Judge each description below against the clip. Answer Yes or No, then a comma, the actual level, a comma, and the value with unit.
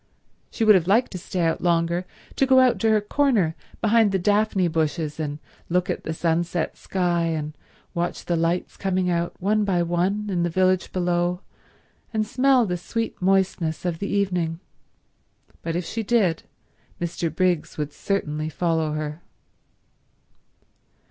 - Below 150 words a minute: No, average, 155 wpm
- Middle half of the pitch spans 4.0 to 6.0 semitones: No, average, 3.3 semitones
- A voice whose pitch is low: No, medium, 180 Hz